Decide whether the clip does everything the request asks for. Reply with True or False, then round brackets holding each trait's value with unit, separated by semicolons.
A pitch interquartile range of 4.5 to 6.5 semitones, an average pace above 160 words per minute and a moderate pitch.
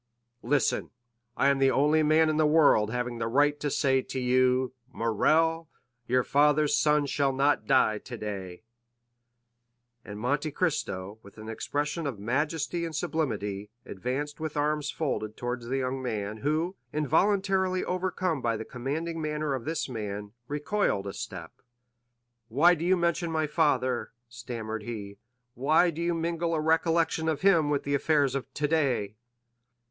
False (4.9 semitones; 155 wpm; 145 Hz)